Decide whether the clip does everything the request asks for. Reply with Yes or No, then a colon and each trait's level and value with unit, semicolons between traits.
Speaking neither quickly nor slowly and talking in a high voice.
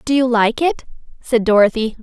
Yes: average, 180 wpm; high, 235 Hz